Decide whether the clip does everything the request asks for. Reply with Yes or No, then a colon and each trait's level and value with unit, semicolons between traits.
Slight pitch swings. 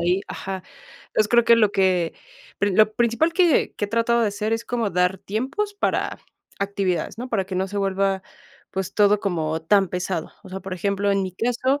No: average, 3.5 semitones